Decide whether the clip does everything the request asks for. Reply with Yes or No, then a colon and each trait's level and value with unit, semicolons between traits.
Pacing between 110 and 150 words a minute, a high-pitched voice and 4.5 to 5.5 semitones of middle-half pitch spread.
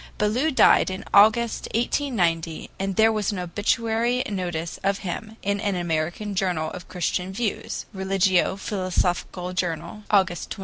No: average, 140 wpm; high, 195 Hz; average, 3.1 semitones